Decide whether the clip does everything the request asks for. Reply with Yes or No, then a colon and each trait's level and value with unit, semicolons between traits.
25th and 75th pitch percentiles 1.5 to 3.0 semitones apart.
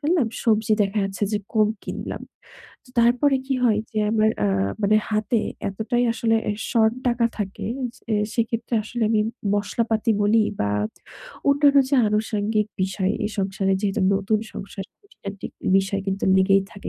Yes: average, 2.7 semitones